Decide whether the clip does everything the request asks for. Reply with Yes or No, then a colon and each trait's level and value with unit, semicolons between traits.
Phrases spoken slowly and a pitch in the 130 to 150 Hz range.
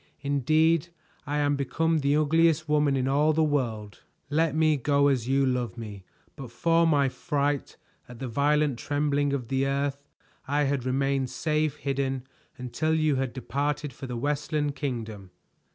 No: average, 160 wpm; medium, 140 Hz